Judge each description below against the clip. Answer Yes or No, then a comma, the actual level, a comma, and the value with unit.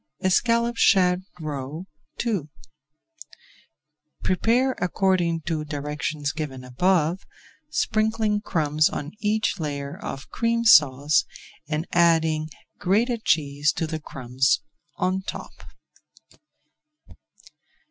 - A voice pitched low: No, medium, 165 Hz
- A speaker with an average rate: No, slow, 90 wpm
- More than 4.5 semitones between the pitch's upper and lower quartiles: Yes, average, 5.2 semitones